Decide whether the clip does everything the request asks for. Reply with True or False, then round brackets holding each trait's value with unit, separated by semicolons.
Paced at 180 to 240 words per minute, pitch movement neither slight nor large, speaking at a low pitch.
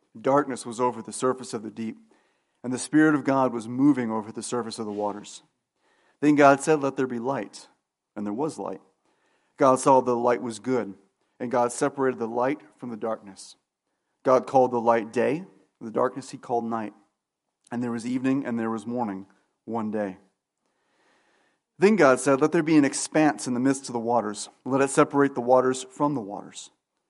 True (200 wpm; 3.2 semitones; 125 Hz)